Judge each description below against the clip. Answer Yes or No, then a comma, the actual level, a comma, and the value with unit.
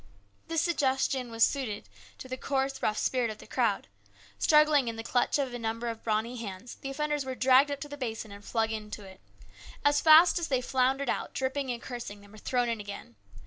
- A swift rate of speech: Yes, fast, 220 wpm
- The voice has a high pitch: Yes, very high, 250 Hz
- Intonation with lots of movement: No, average, 3.7 semitones